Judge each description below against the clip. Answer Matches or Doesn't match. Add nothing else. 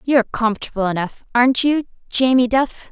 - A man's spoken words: Doesn't match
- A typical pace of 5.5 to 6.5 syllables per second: Matches